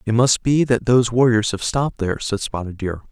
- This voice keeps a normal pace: No, fast, 230 wpm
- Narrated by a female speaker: No, male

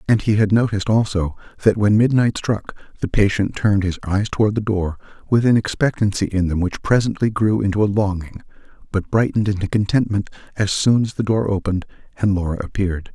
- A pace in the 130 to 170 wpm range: No, average, 185 wpm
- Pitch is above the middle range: No, low, 100 Hz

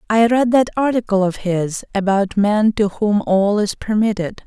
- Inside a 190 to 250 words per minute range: No, average, 175 wpm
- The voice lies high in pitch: Yes, high, 210 Hz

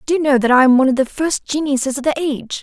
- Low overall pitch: No, very high, 275 Hz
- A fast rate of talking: Yes, fast, 320 wpm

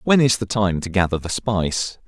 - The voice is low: Yes, low, 100 Hz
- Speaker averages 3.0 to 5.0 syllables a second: No, 5.2 syllables/s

